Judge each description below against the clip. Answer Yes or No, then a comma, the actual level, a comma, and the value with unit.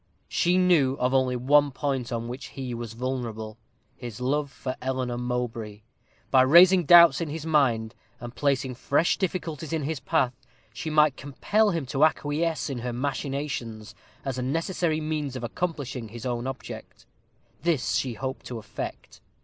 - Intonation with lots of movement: No, average, 4.0 semitones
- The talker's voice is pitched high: No, low, 135 Hz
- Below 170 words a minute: Yes, average, 160 wpm